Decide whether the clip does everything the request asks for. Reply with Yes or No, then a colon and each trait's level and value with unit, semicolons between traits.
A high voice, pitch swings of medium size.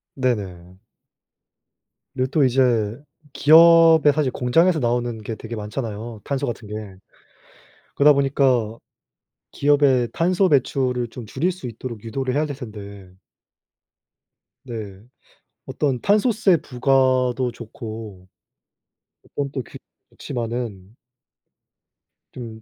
No: low, 125 Hz; average, 4.0 semitones